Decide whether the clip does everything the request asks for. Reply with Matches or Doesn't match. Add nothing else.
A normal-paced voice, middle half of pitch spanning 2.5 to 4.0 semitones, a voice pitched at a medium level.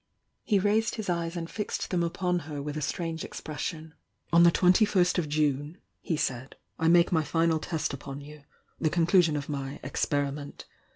Matches